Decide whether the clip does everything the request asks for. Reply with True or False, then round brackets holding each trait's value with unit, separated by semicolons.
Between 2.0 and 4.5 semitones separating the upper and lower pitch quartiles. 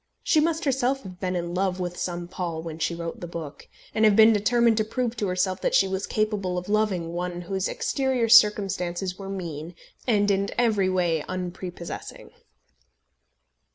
True (3.5 semitones)